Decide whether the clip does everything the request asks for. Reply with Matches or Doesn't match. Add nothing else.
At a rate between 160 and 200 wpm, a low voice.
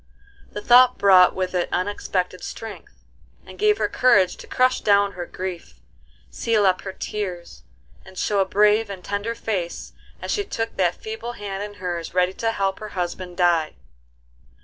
Doesn't match